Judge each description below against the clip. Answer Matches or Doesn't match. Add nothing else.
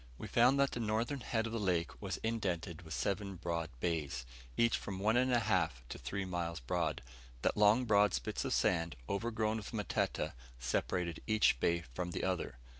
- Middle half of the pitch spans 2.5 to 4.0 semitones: Doesn't match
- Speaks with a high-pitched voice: Doesn't match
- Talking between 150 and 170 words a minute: Doesn't match